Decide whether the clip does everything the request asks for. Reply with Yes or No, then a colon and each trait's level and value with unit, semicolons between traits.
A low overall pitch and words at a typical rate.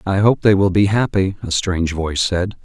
No: very low, 95 Hz; fast, 225 wpm